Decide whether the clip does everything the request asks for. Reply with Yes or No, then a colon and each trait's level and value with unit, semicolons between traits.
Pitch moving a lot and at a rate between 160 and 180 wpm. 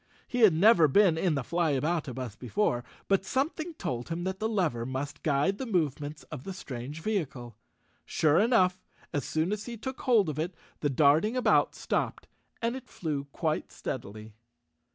Yes: wide, 6.8 semitones; average, 170 wpm